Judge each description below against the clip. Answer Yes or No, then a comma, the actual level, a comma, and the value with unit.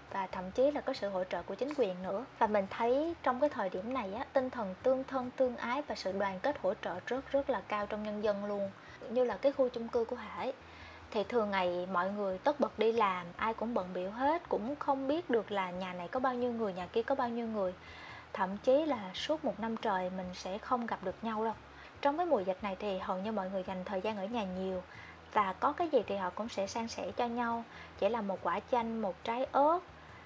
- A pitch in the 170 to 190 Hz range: No, high, 220 Hz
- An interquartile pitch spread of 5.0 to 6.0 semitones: Yes, average, 5.3 semitones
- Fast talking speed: Yes, fast, 260 wpm